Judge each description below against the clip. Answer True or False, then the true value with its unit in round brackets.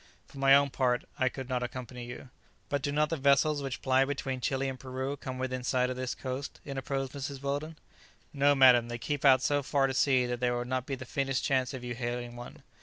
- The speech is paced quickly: True (235 wpm)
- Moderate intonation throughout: False (1.8 semitones)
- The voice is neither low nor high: False (130 Hz)